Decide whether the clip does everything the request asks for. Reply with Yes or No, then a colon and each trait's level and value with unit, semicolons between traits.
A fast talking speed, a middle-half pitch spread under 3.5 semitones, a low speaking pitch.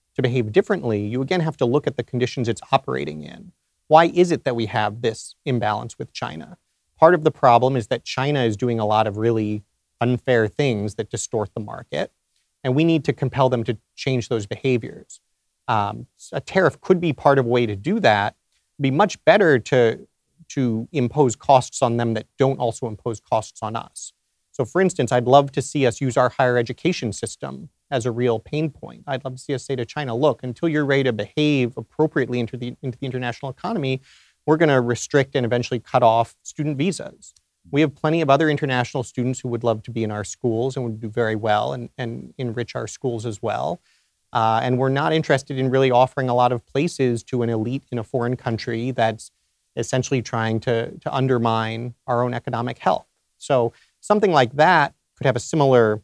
Yes: fast, 210 wpm; average, 3.1 semitones; low, 125 Hz